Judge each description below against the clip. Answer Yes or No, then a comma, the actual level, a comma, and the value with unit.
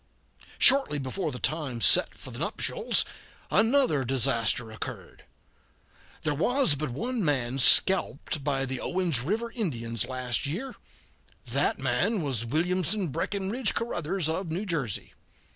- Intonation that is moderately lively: No, wide, 7.1 semitones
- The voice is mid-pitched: Yes, medium, 155 Hz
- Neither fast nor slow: No, slow, 125 wpm